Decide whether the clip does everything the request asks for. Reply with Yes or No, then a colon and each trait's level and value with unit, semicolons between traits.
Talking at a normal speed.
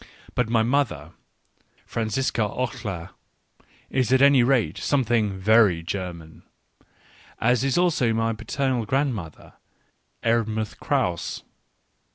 No: slow, 100 wpm